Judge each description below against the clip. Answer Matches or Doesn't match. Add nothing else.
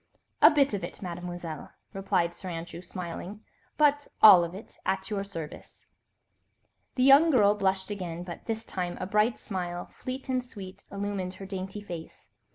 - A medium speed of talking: Matches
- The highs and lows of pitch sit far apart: Doesn't match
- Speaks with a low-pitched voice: Doesn't match